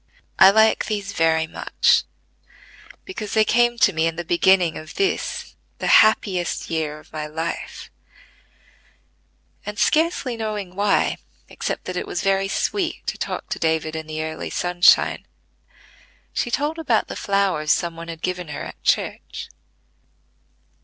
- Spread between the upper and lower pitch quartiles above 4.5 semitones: Yes, average, 5.0 semitones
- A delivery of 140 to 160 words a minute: Yes, average, 145 wpm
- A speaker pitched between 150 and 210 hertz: Yes, medium, 185 Hz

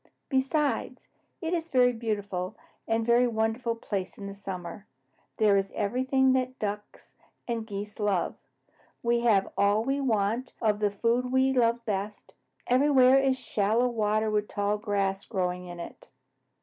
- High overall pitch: Yes, high, 220 Hz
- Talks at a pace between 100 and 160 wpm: Yes, average, 150 wpm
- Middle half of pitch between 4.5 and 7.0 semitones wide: No, average, 3.7 semitones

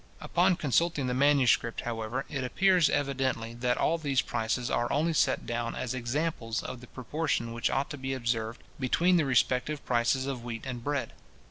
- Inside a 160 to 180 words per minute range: Yes, average, 175 wpm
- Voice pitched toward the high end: No, low, 130 Hz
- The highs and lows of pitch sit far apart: No, average, 3.6 semitones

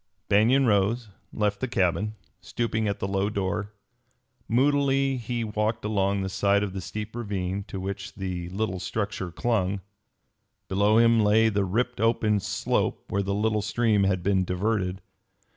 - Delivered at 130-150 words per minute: No, average, 160 wpm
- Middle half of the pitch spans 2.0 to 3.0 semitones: Yes, narrow, 2.5 semitones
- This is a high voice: No, low, 105 Hz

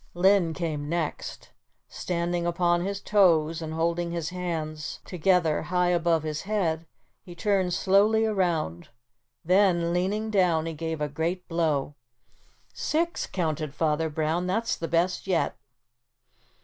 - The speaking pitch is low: No, medium, 170 Hz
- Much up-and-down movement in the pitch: No, narrow, 2.5 semitones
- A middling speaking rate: No, slow, 130 wpm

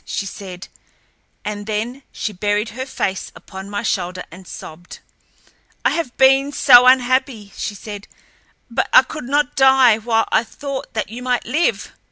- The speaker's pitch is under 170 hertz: No, high, 230 Hz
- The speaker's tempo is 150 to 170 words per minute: Yes, average, 160 wpm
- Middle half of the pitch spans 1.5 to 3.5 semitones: No, average, 4.3 semitones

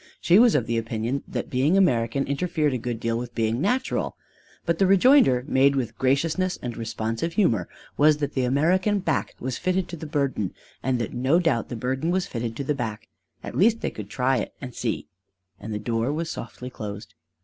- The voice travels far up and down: Yes, wide, 6.2 semitones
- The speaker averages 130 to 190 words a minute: No, fast, 205 wpm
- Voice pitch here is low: Yes, low, 130 Hz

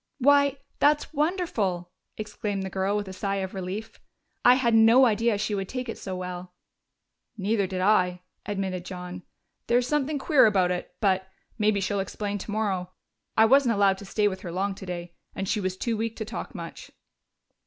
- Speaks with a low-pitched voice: No, high, 205 Hz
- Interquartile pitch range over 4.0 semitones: No, average, 3.4 semitones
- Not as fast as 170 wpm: No, average, 185 wpm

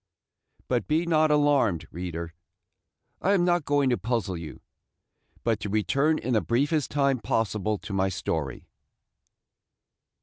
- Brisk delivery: No, slow, 135 wpm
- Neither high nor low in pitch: No, low, 120 Hz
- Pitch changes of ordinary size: No, wide, 7.1 semitones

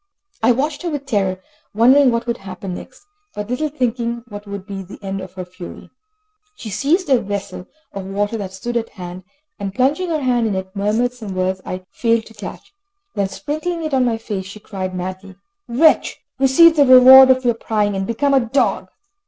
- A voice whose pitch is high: Yes, high, 225 Hz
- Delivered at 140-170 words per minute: No, average, 200 wpm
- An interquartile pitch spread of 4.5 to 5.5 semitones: Yes, average, 5.2 semitones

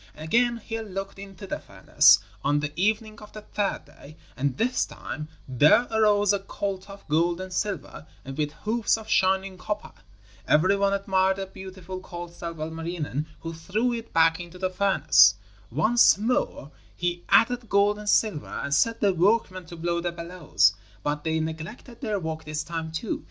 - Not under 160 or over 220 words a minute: Yes, average, 175 wpm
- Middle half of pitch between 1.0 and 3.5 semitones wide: No, average, 4.4 semitones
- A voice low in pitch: No, medium, 185 Hz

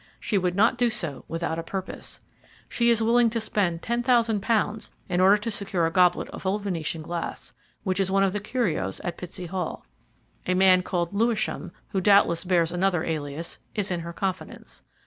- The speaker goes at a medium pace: Yes, average, 190 wpm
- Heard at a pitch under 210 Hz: Yes, high, 190 Hz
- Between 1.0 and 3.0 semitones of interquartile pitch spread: No, average, 3.5 semitones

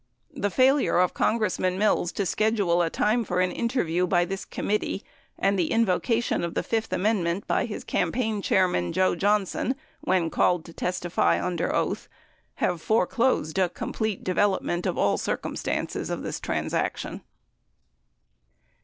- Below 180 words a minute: Yes, average, 145 wpm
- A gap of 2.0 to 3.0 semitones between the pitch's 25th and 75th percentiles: No, average, 3.7 semitones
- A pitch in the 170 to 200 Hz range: Yes, high, 190 Hz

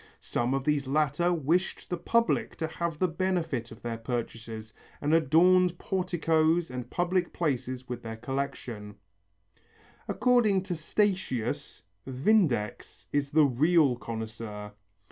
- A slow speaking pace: Yes, slow, 125 wpm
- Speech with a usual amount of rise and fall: No, wide, 6.5 semitones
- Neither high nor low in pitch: Yes, medium, 150 Hz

